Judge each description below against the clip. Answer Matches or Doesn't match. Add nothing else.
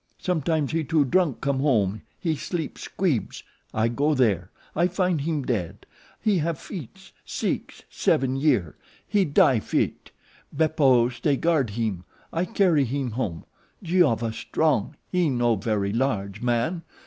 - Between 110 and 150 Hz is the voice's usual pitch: Matches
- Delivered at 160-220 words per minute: Doesn't match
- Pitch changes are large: Matches